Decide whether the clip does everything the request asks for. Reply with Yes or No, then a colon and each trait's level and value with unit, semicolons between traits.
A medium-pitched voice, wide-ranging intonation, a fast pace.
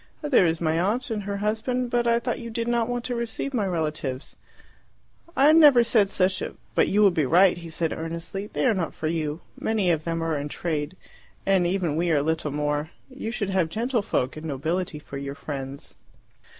Yes: medium, 180 Hz; wide, 6.1 semitones; fast, 210 wpm